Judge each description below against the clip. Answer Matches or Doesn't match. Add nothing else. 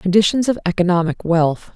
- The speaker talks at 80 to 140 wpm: Matches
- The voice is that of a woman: Matches